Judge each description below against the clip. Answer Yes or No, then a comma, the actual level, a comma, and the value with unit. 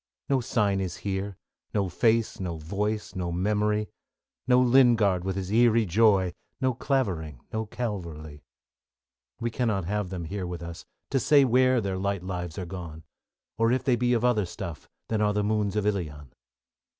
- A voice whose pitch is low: Yes, low, 100 Hz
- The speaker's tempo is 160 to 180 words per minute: Yes, average, 175 wpm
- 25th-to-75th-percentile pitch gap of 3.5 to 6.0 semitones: Yes, average, 4.3 semitones